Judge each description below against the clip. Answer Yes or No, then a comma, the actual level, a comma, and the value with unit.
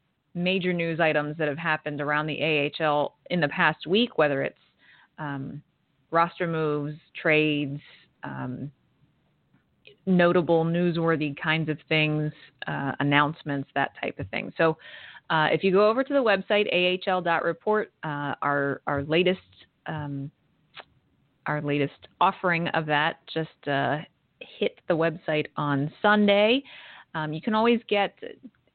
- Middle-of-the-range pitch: Yes, medium, 155 Hz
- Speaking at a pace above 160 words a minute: No, slow, 135 wpm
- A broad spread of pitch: No, average, 3.6 semitones